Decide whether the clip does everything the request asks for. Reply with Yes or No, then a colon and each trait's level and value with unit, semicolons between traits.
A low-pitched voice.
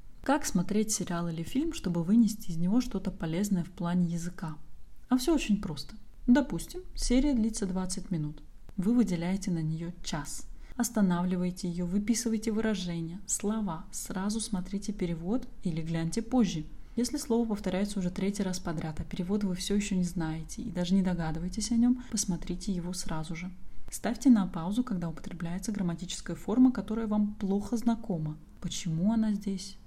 No: high, 195 Hz